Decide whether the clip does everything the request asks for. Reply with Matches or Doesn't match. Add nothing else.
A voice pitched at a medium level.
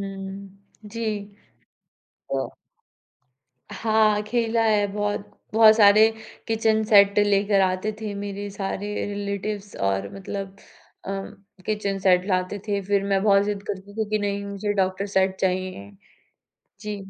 Doesn't match